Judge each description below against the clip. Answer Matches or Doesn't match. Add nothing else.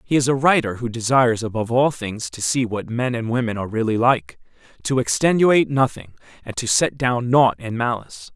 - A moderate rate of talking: Matches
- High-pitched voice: Doesn't match